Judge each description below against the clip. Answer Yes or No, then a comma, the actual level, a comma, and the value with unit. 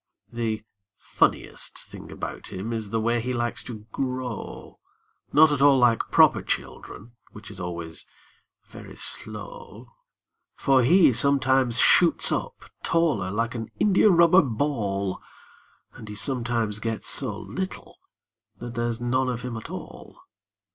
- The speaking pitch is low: Yes, low, 120 Hz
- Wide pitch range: No, average, 3.8 semitones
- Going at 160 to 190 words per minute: No, slow, 135 wpm